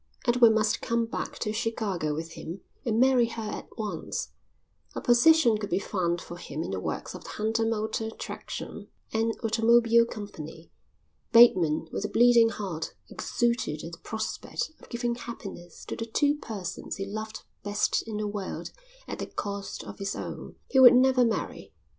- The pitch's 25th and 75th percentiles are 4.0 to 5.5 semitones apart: No, average, 3.1 semitones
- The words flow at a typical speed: Yes, average, 170 wpm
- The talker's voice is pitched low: No, high, 220 Hz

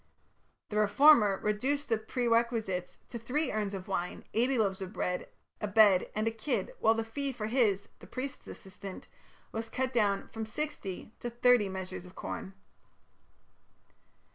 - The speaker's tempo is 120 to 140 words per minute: No, average, 155 wpm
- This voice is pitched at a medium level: No, high, 220 Hz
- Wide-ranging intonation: No, average, 3.8 semitones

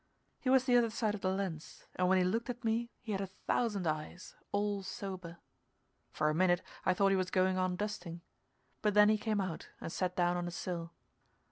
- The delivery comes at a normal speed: No, fast, 220 wpm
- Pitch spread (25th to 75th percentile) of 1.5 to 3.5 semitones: Yes, average, 2.9 semitones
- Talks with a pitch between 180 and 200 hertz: Yes, high, 190 Hz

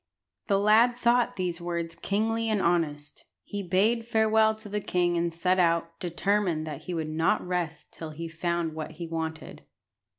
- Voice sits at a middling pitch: Yes, medium, 175 Hz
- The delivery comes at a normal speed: Yes, average, 175 wpm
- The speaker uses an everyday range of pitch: Yes, average, 4.0 semitones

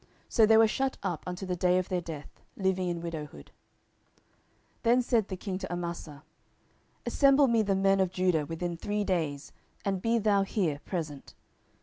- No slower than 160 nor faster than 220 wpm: Yes, average, 180 wpm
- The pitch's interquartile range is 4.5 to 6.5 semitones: No, average, 3.5 semitones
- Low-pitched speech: No, medium, 185 Hz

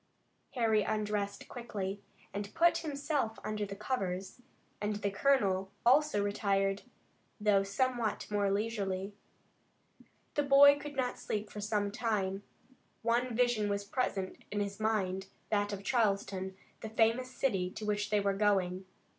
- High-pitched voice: Yes, high, 210 Hz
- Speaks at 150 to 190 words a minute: No, average, 140 wpm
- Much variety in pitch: No, average, 3.0 semitones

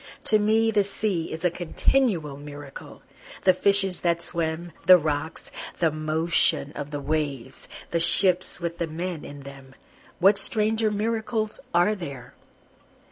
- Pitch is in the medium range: Yes, medium, 170 Hz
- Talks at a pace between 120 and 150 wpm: Yes, average, 140 wpm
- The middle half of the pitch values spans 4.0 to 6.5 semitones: Yes, average, 4.8 semitones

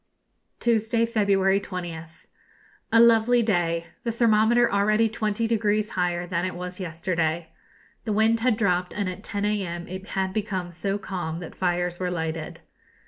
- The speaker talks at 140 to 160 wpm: Yes, average, 150 wpm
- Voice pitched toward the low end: No, high, 195 Hz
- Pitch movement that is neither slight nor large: Yes, average, 3.7 semitones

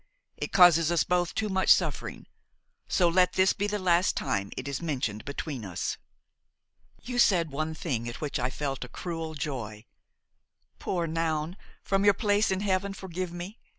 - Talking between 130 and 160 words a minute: No, average, 170 wpm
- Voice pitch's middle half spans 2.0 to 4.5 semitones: No, average, 4.9 semitones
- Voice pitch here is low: No, medium, 170 Hz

